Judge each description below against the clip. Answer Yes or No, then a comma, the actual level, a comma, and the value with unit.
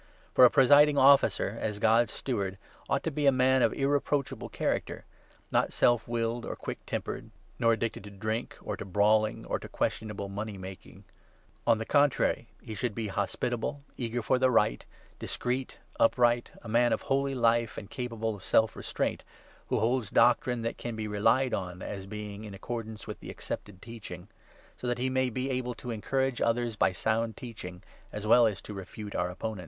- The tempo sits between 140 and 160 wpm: No, average, 190 wpm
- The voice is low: Yes, low, 115 Hz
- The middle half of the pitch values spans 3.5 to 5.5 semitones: No, average, 2.9 semitones